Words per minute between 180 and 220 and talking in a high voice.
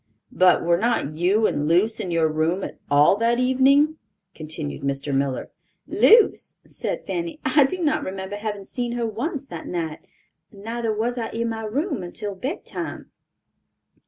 No: average, 160 wpm; high, 215 Hz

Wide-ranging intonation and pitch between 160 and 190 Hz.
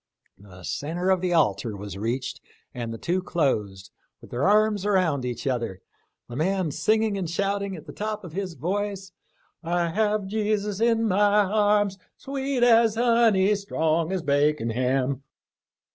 Yes: wide, 6.7 semitones; medium, 185 Hz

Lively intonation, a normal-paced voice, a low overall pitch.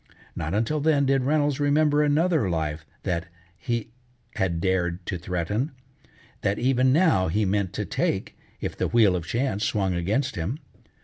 Yes: wide, 7.7 semitones; average, 160 wpm; low, 110 Hz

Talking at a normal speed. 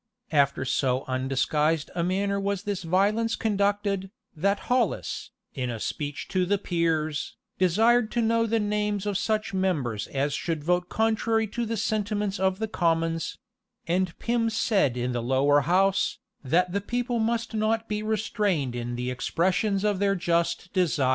Yes: average, 160 wpm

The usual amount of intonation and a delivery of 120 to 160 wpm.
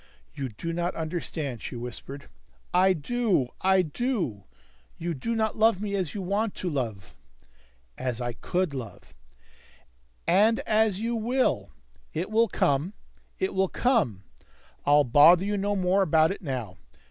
No: wide, 7.7 semitones; average, 150 wpm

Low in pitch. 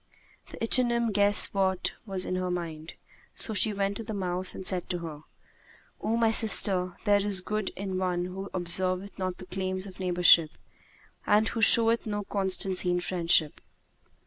No: high, 190 Hz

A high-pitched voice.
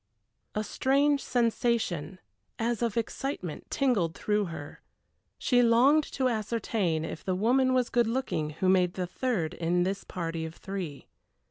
Yes: high, 215 Hz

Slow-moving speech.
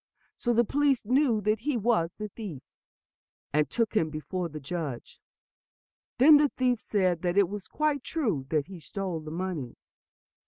No: average, 165 wpm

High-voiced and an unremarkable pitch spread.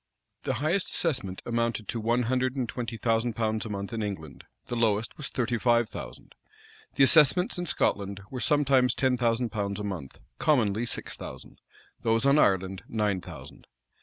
No: low, 115 Hz; average, 3.6 semitones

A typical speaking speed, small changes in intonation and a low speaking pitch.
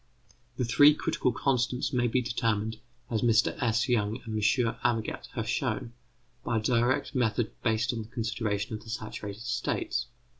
Yes: average, 160 wpm; narrow, 2.0 semitones; low, 115 Hz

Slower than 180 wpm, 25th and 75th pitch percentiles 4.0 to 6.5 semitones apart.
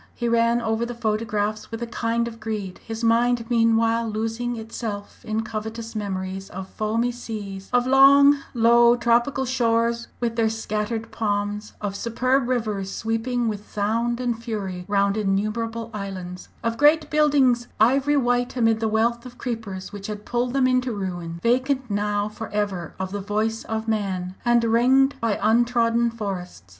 No: average, 160 wpm; narrow, 2.4 semitones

